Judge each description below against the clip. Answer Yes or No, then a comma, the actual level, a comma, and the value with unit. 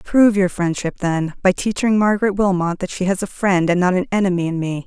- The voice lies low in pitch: No, medium, 185 Hz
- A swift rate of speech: Yes, fast, 235 wpm